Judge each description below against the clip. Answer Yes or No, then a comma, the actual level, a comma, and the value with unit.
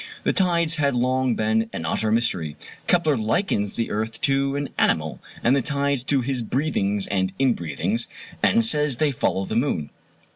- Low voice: Yes, low, 120 Hz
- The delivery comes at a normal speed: Yes, average, 170 wpm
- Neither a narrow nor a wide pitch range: Yes, average, 5.0 semitones